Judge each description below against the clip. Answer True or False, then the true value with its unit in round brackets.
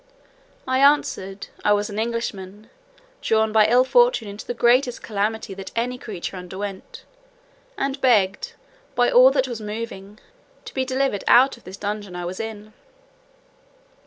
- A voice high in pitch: True (220 Hz)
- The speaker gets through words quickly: False (155 wpm)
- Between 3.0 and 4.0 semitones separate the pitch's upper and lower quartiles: True (3.7 semitones)